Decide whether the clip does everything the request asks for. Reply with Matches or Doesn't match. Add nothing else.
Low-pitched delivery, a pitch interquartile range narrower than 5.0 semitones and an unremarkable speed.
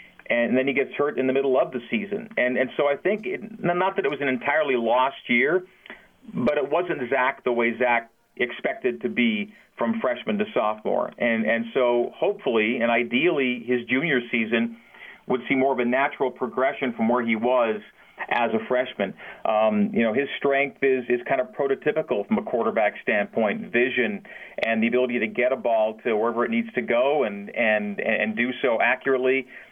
Matches